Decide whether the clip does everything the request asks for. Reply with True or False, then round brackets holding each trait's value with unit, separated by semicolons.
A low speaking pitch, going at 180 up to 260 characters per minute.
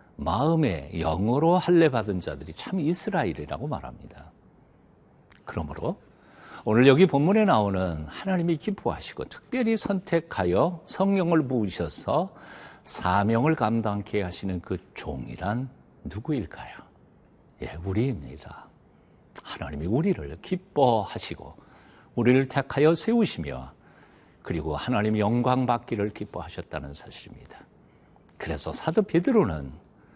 False (120 Hz; 275 characters per minute)